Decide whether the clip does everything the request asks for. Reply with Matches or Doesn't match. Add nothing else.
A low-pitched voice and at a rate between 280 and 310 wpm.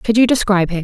Doesn't match